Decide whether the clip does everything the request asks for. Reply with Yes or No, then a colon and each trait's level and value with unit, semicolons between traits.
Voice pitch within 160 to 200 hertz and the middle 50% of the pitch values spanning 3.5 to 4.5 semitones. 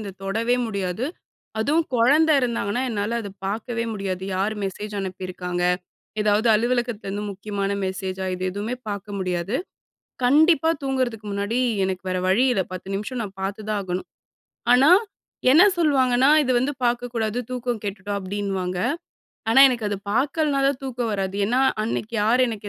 No: high, 215 Hz; average, 4.1 semitones